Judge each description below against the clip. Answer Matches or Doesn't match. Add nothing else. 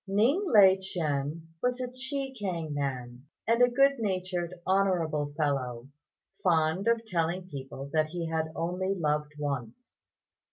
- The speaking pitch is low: Doesn't match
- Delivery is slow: Matches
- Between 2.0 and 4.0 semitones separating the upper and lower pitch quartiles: Doesn't match